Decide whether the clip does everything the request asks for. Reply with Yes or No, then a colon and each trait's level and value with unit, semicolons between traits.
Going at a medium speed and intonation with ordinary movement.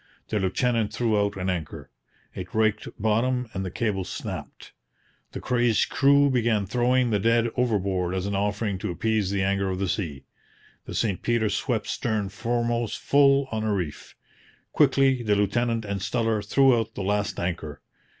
Yes: average, 170 wpm; average, 3.4 semitones